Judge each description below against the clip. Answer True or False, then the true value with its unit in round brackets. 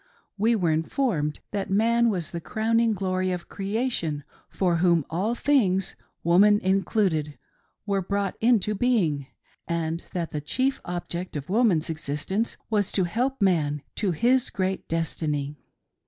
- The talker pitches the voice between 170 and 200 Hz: True (185 Hz)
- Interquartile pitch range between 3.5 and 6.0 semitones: True (4.9 semitones)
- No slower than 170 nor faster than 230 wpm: False (145 wpm)